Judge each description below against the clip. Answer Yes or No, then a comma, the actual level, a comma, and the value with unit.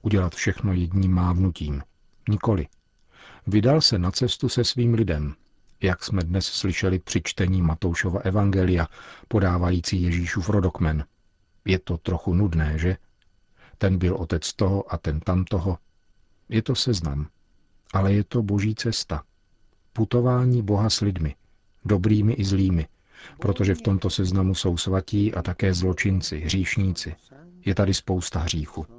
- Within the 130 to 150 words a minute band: Yes, average, 135 wpm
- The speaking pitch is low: Yes, very low, 95 Hz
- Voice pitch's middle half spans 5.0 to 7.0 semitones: No, average, 2.7 semitones